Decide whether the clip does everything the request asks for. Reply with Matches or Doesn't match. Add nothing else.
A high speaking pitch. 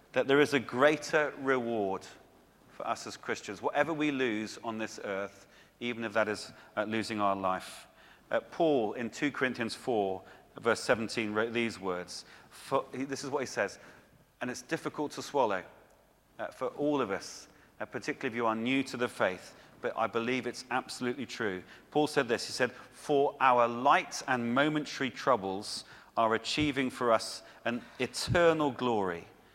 Doesn't match